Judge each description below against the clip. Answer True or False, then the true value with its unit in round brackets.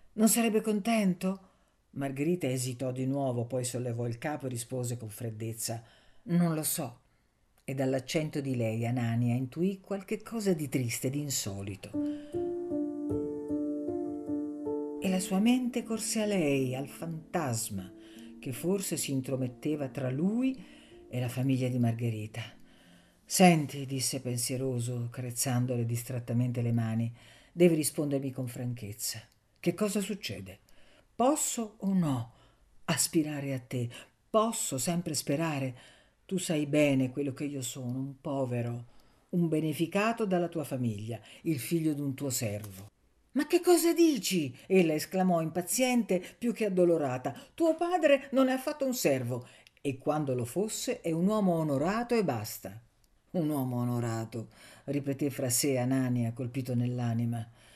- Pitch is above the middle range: False (140 Hz)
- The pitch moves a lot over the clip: True (7.2 semitones)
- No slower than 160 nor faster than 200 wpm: False (135 wpm)